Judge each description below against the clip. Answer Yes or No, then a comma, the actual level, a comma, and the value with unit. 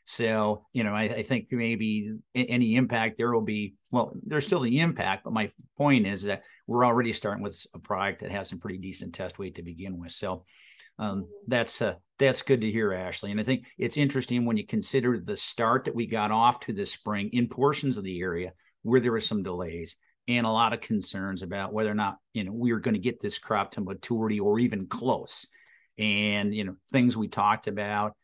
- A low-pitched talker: Yes, low, 110 Hz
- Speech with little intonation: No, average, 3.0 semitones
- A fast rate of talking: Yes, fast, 220 wpm